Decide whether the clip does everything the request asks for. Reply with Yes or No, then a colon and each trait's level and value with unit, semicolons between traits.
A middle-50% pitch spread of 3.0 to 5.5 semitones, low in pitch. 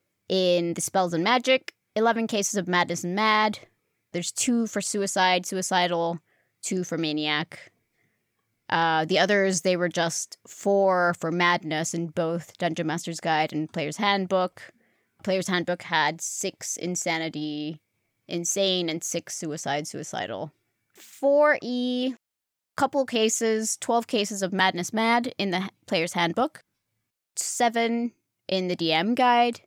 No: average, 4.4 semitones; medium, 180 Hz